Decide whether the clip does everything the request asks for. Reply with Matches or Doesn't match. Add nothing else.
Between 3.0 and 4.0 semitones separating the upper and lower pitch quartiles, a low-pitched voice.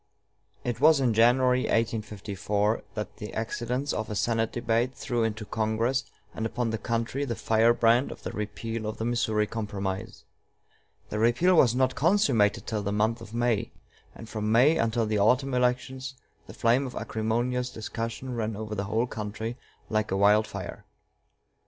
Doesn't match